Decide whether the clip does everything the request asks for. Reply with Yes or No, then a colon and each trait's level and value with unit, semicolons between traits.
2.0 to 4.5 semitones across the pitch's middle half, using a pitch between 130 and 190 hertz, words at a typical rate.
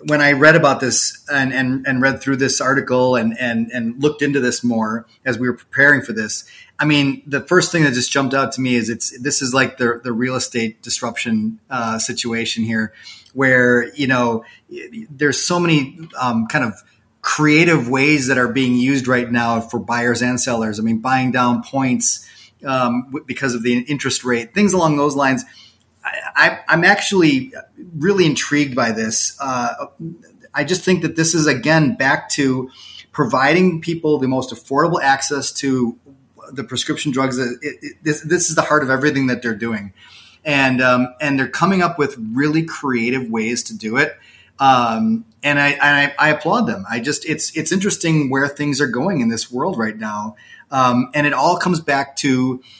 Yes: average, 3.7 semitones; low, 135 Hz; average, 190 wpm